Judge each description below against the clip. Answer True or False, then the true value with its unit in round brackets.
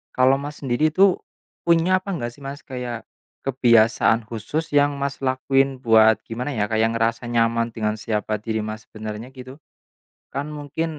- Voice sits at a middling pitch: False (120 Hz)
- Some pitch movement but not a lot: True (3.7 semitones)